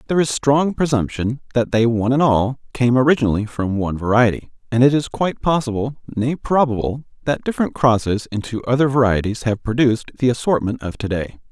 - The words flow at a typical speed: Yes, average, 175 wpm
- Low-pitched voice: Yes, low, 125 Hz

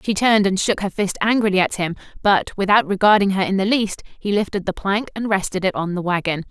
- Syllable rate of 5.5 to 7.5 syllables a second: Yes, 6.0 syllables/s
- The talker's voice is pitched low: No, high, 195 Hz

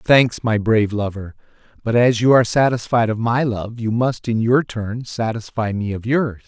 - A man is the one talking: Yes, male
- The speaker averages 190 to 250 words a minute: Yes, average, 195 wpm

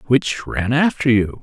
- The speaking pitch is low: Yes, low, 125 Hz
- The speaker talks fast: No, average, 170 wpm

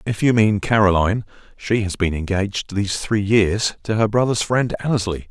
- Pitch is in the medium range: No, low, 105 Hz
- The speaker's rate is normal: Yes, average, 180 wpm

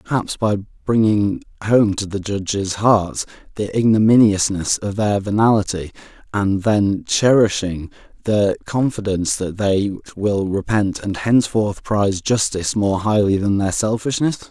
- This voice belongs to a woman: No, male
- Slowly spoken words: Yes, slow, 130 wpm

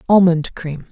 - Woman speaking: Yes, female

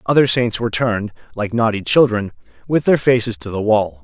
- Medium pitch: No, low, 110 Hz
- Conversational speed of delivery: Yes, average, 195 wpm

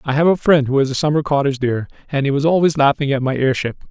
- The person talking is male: Yes, male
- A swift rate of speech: Yes, fast, 275 wpm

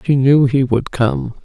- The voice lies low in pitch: Yes, low, 130 Hz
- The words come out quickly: Yes, fast, 210 wpm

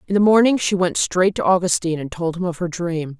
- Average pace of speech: No, fast, 265 wpm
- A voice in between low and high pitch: Yes, medium, 180 Hz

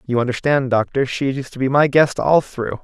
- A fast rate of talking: Yes, fast, 235 wpm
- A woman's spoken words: No, male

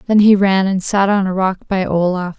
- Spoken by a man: No, female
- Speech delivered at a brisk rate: Yes, fast, 250 wpm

